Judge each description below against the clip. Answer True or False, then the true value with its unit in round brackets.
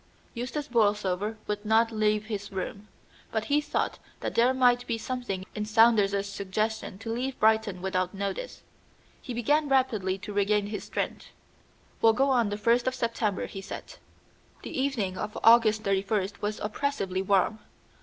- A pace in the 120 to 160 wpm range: True (155 wpm)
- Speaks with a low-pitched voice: False (215 Hz)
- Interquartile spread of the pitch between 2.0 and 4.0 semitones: True (3.1 semitones)